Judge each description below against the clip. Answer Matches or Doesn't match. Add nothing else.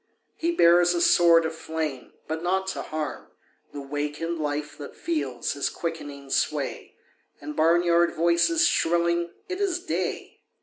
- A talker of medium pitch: Matches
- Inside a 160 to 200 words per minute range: Doesn't match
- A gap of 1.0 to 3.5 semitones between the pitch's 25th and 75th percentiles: Matches